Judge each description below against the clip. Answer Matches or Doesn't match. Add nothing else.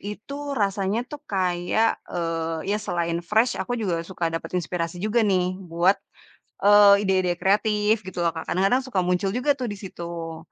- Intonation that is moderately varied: Matches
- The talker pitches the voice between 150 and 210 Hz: Matches